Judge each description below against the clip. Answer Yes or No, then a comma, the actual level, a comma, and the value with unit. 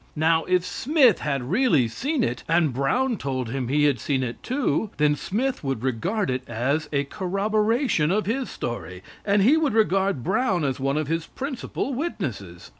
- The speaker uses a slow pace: No, average, 180 wpm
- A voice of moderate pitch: Yes, medium, 165 Hz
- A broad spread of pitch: Yes, wide, 8.7 semitones